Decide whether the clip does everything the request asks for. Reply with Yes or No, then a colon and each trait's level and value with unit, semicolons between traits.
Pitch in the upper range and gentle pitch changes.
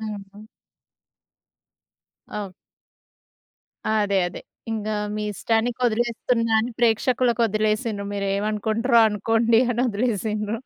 Yes: high, 220 Hz; narrow, 1.9 semitones